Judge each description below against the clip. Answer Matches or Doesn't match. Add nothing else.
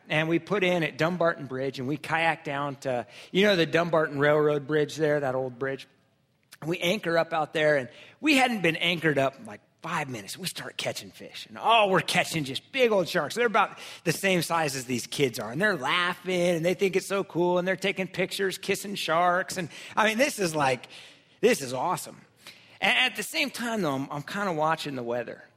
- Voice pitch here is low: Doesn't match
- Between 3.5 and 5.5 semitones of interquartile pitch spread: Matches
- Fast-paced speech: Matches